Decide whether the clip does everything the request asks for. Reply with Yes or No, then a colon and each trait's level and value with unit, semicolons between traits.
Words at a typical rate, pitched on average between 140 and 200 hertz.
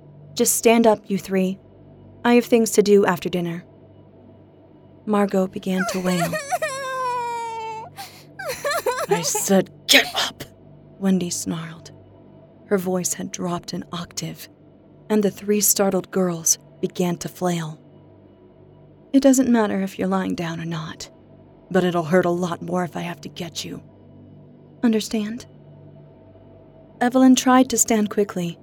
No: slow, 130 wpm; high, 190 Hz